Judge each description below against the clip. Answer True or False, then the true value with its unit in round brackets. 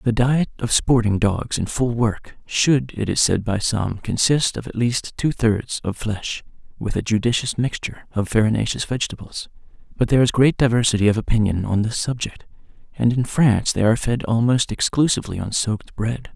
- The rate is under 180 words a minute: False (185 wpm)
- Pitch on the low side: True (115 Hz)